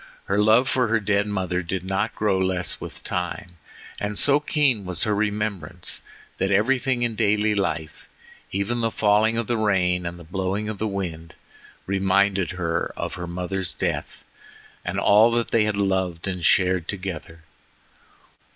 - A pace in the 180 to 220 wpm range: No, average, 165 wpm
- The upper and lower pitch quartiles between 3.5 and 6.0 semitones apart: No, average, 2.9 semitones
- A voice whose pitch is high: No, low, 100 Hz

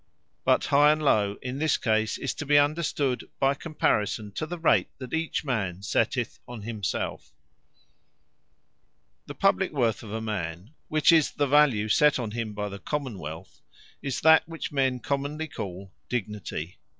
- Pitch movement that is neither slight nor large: No, wide, 5.9 semitones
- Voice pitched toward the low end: Yes, low, 125 Hz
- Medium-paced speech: Yes, average, 165 wpm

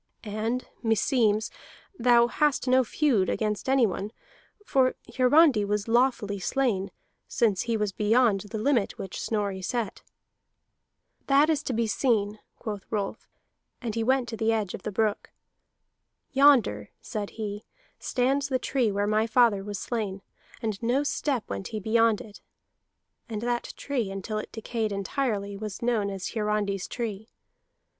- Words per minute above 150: No, average, 145 wpm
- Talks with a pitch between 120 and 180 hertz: No, high, 220 Hz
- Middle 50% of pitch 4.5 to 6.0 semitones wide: No, average, 3.3 semitones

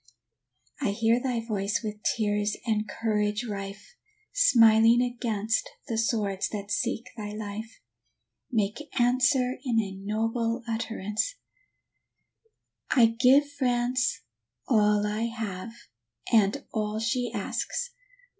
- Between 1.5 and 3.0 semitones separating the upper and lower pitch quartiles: Yes, narrow, 2.6 semitones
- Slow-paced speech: Yes, slow, 110 wpm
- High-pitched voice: Yes, high, 225 Hz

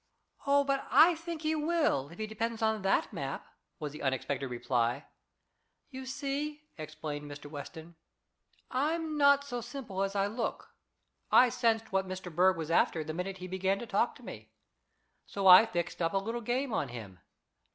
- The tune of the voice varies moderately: No, wide, 8.9 semitones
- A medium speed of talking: Yes, average, 175 wpm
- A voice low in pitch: No, high, 195 Hz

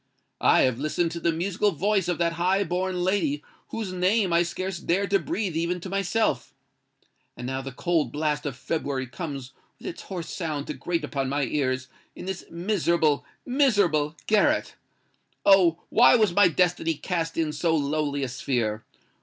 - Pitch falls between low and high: Yes, medium, 170 Hz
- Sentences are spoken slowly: No, average, 165 wpm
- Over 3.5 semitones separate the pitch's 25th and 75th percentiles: Yes, average, 4.3 semitones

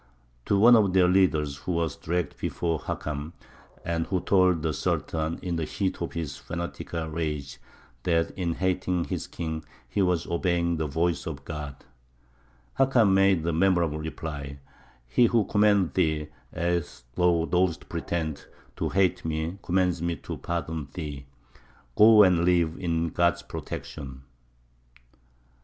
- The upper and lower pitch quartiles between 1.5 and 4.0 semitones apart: Yes, average, 2.7 semitones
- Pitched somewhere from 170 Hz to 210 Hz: No, very low, 85 Hz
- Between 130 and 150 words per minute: Yes, average, 145 wpm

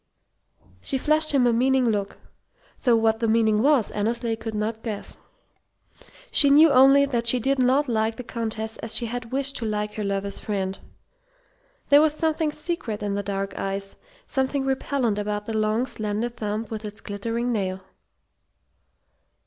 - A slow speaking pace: No, average, 165 wpm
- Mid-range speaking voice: No, high, 230 Hz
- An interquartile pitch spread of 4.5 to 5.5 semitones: No, average, 4.0 semitones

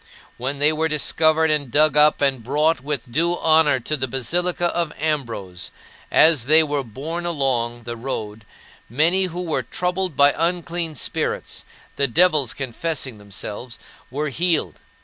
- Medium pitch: Yes, medium, 150 Hz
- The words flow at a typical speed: Yes, average, 150 wpm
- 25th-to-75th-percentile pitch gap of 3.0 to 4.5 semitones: Yes, average, 4.2 semitones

